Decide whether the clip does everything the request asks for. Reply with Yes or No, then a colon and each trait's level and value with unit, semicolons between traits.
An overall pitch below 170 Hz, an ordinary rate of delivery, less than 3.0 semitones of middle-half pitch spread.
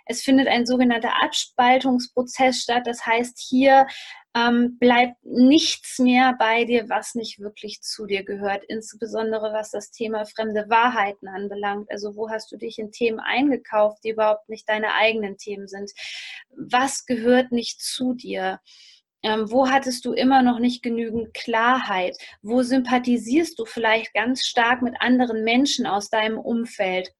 No: high, 235 Hz; average, 150 wpm; narrow, 2.6 semitones